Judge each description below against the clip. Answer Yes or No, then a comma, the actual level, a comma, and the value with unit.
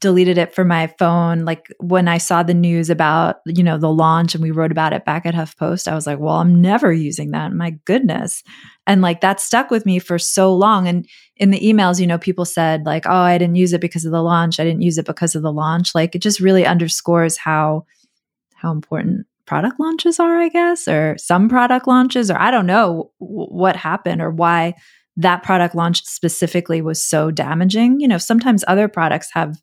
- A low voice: No, medium, 175 Hz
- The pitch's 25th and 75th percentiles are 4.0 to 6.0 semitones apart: No, average, 3.0 semitones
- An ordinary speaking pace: No, fast, 220 wpm